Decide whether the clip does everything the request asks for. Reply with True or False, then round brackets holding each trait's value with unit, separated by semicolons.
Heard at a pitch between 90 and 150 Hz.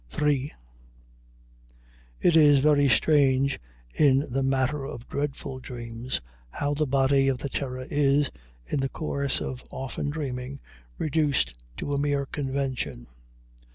True (140 Hz)